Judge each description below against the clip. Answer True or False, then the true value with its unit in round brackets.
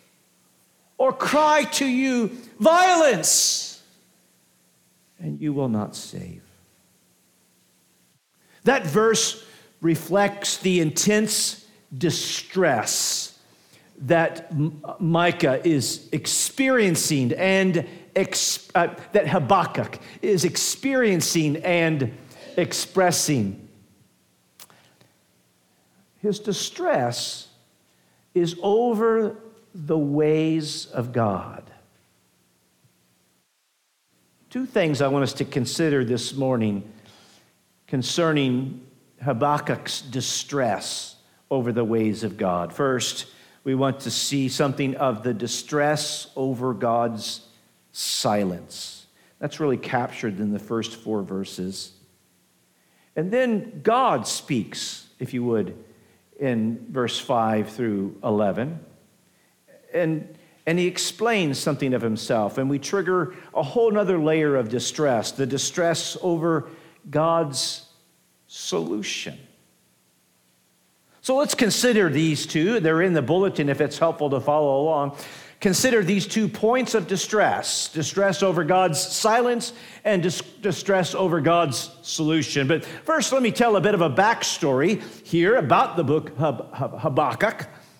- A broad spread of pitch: True (7.5 semitones)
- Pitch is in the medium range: True (155 Hz)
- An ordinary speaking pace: False (105 wpm)